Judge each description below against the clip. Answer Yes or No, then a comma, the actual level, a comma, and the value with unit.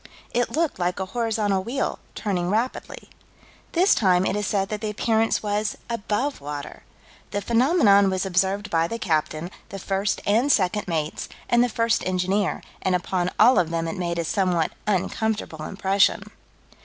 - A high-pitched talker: Yes, high, 200 Hz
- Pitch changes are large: No, average, 3.6 semitones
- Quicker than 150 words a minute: Yes, average, 165 wpm